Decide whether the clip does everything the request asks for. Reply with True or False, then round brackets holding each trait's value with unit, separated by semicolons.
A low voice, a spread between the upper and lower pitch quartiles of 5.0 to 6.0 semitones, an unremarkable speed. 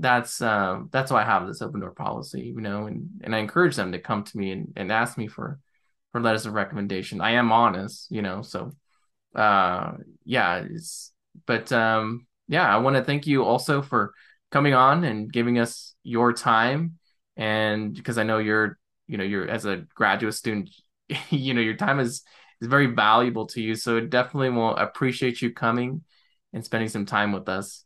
False (115 Hz; 3.1 semitones; 195 wpm)